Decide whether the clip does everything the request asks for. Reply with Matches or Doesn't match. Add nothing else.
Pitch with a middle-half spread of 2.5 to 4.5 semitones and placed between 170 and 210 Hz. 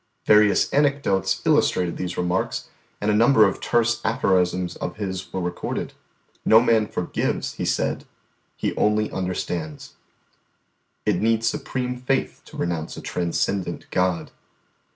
Doesn't match